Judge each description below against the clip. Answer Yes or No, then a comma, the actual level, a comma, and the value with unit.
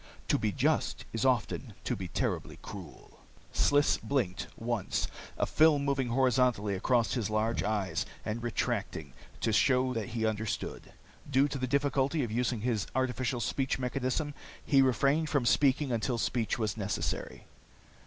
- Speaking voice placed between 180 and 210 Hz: No, low, 125 Hz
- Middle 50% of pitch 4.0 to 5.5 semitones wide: No, average, 3.5 semitones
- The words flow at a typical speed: Yes, average, 150 wpm